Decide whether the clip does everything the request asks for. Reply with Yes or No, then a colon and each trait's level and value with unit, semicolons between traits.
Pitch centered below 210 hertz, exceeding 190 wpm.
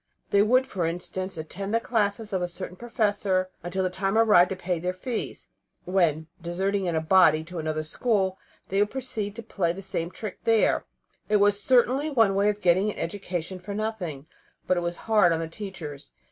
Yes: high, 190 Hz; average, 200 wpm